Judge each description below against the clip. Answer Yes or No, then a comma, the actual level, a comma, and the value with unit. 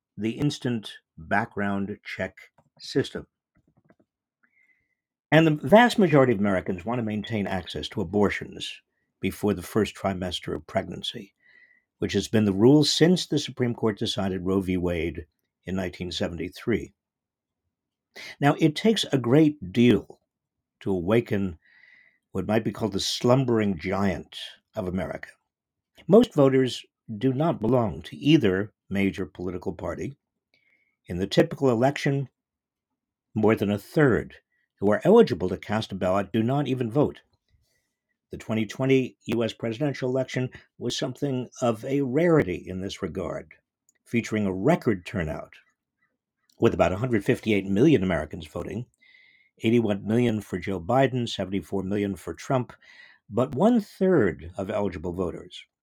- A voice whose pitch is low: Yes, low, 110 Hz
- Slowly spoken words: Yes, slow, 130 wpm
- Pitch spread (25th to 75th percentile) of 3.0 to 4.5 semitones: No, wide, 5.4 semitones